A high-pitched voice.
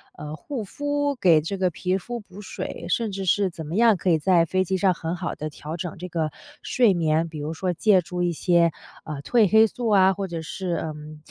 No: medium, 180 Hz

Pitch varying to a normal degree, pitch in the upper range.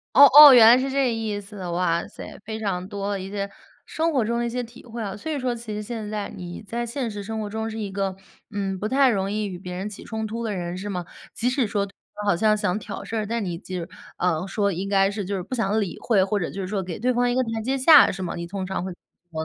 Yes: average, 3.3 semitones; high, 210 Hz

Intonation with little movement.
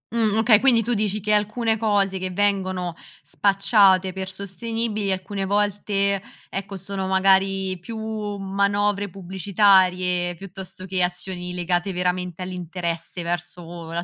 Yes: narrow, 2.1 semitones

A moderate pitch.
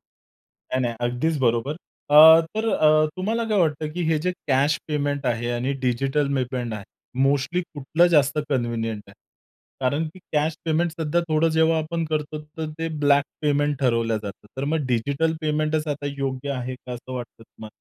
Yes: medium, 145 Hz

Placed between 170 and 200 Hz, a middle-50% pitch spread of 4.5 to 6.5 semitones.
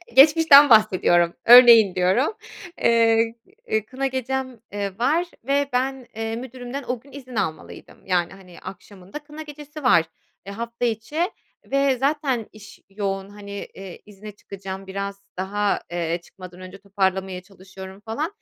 No: high, 220 Hz; average, 5.3 semitones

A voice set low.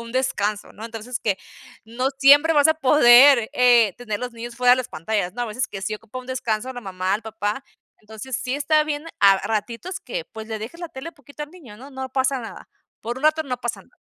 No: high, 245 Hz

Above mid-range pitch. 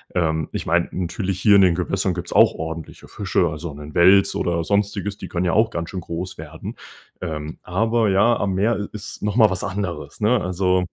No: very low, 95 Hz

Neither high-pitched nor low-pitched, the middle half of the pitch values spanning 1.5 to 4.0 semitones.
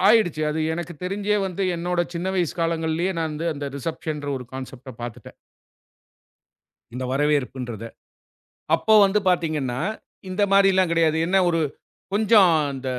No: medium, 165 Hz; average, 4.6 semitones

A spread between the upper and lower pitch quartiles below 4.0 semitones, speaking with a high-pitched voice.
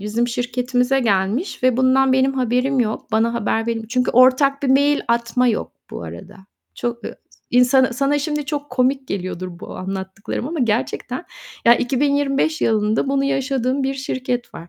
Yes: average, 2.8 semitones; very high, 250 Hz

